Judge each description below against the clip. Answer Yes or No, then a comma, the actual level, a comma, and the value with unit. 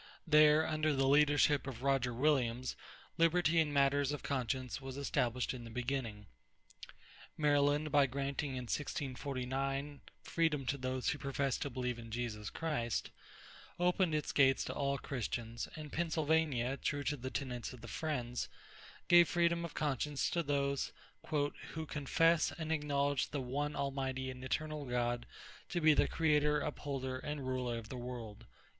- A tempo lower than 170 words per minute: Yes, average, 150 wpm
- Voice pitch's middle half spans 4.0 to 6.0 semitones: No, average, 2.8 semitones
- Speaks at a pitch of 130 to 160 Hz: Yes, medium, 140 Hz